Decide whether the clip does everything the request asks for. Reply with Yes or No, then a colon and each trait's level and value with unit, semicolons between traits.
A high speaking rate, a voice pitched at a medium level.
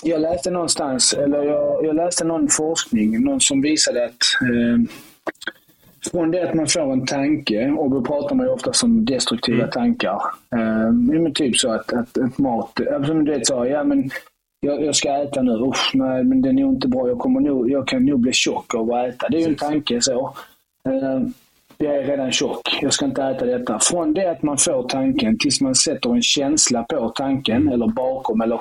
Yes: fast, 210 wpm; medium, 160 Hz